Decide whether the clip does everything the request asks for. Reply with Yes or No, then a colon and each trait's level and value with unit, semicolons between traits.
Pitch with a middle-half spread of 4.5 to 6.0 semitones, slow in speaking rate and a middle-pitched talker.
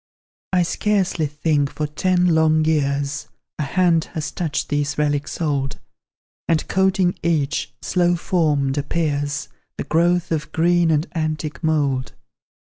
No: average, 2.9 semitones; slow, 130 wpm; medium, 155 Hz